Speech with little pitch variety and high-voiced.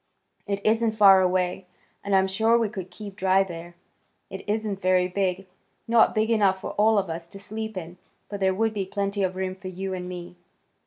Yes: narrow, 2.2 semitones; high, 195 Hz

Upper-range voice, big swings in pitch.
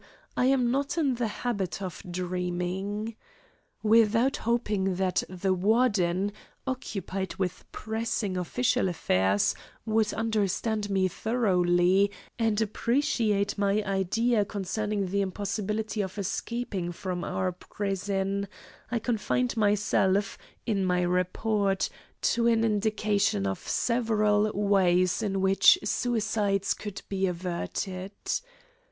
No: high, 200 Hz; average, 2.9 semitones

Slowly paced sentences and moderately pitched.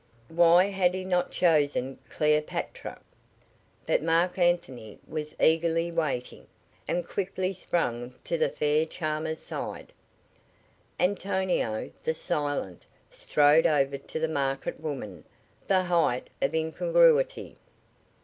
Yes: slow, 110 wpm; medium, 160 Hz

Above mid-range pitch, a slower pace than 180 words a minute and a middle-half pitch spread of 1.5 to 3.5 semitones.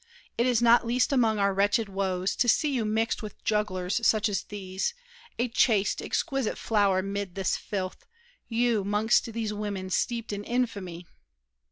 Yes: high, 210 Hz; average, 160 wpm; average, 3.0 semitones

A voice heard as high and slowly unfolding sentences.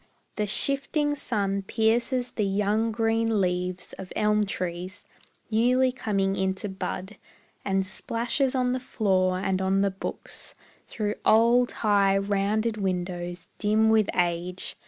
Yes: high, 205 Hz; slow, 130 wpm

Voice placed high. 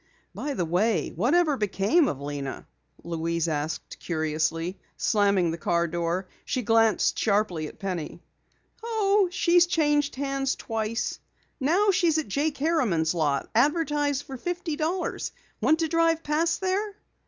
Yes: very high, 255 Hz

